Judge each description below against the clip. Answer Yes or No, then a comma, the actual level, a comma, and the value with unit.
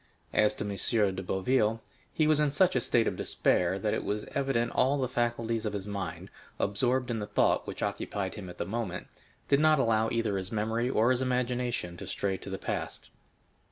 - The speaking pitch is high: No, low, 115 Hz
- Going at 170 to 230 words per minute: Yes, fast, 205 wpm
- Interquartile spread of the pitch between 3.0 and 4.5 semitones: Yes, average, 4.1 semitones